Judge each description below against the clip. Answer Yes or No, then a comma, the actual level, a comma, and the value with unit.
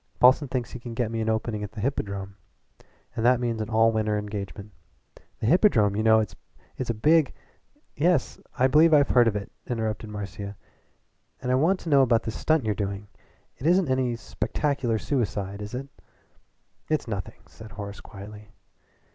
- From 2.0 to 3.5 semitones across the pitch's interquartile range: No, average, 4.0 semitones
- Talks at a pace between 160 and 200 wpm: Yes, average, 180 wpm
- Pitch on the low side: Yes, low, 115 Hz